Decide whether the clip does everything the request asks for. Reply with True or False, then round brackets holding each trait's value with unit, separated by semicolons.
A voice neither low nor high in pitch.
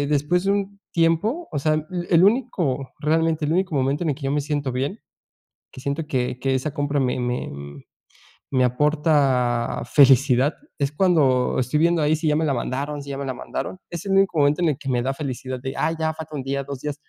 True (145 Hz)